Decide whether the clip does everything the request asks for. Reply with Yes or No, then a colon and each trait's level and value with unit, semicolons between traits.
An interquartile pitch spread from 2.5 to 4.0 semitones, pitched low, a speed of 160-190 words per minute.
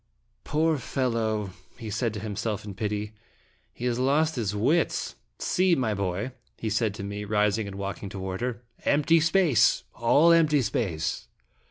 No: average, 5.1 semitones; low, 110 Hz; average, 170 wpm